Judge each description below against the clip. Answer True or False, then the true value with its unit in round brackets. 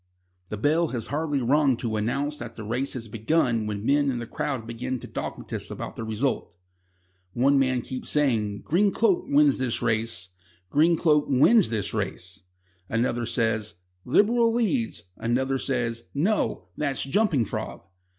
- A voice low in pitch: True (130 Hz)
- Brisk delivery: False (155 wpm)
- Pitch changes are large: False (4.7 semitones)